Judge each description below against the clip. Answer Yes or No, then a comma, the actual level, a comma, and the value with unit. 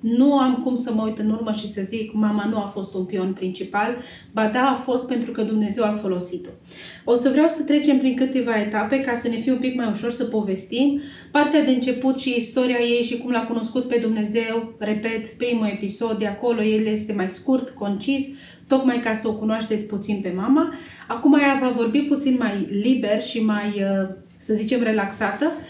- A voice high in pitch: Yes, high, 230 Hz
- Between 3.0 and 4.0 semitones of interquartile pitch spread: Yes, average, 3.3 semitones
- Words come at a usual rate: No, fast, 205 wpm